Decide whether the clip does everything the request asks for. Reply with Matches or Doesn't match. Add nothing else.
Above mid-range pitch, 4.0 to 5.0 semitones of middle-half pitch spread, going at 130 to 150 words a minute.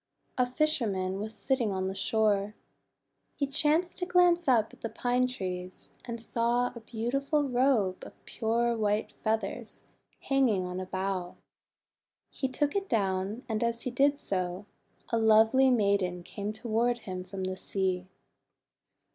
Matches